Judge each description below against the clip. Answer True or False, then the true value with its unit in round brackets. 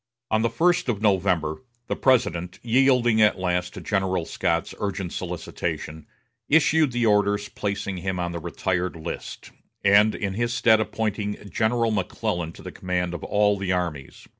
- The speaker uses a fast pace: False (160 wpm)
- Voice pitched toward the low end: True (100 Hz)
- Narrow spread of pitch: False (3.7 semitones)